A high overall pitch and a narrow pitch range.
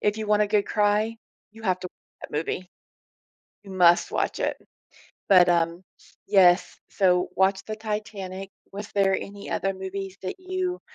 Yes: high, 195 Hz; narrow, 2.2 semitones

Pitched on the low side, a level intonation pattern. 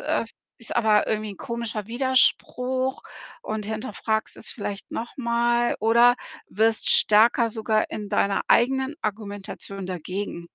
No: high, 220 Hz; narrow, 2.3 semitones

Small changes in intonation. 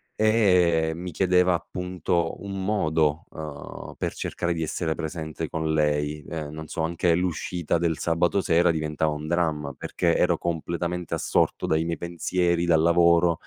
Yes: narrow, 1.9 semitones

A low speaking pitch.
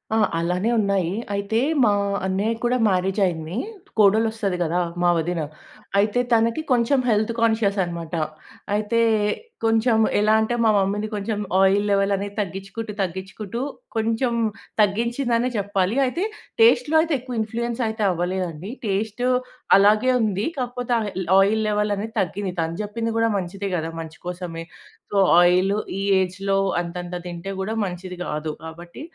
No: high, 205 Hz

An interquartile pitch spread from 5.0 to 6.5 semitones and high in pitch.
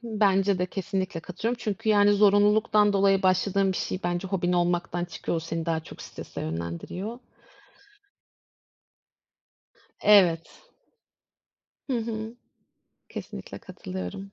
No: average, 2.9 semitones; high, 195 Hz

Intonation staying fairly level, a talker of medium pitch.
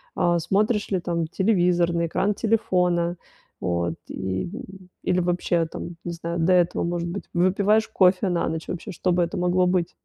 Yes: narrow, 1.6 semitones; medium, 175 Hz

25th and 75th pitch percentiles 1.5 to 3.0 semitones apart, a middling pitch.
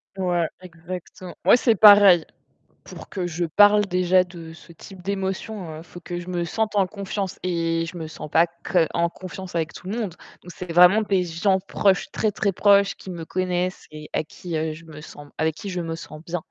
Yes: average, 2.7 semitones; medium, 180 Hz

